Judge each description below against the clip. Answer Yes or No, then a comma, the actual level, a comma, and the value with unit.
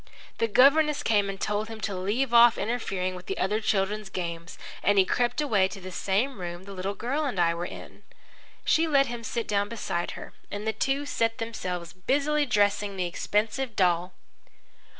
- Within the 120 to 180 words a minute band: No, average, 190 wpm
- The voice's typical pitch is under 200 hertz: No, high, 205 Hz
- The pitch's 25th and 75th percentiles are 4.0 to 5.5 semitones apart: Yes, average, 4.4 semitones